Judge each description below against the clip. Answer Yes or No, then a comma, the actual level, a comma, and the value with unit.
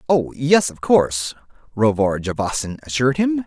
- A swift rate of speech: No, average, 140 wpm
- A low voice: Yes, low, 130 Hz